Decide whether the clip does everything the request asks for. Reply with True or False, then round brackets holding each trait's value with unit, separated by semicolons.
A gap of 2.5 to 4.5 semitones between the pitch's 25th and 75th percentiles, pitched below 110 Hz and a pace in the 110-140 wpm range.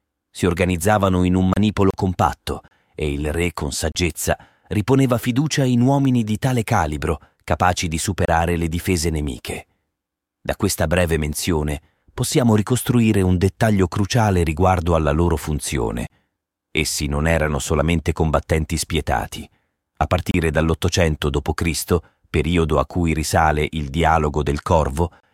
True (3.9 semitones; 85 Hz; 130 wpm)